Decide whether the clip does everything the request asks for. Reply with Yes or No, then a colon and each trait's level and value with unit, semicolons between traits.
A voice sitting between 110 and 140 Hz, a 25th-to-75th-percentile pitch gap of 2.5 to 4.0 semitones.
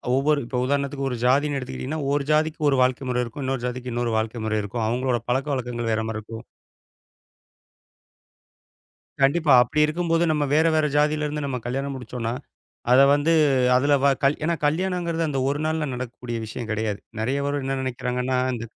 Yes: low, 135 Hz; average, 3.4 semitones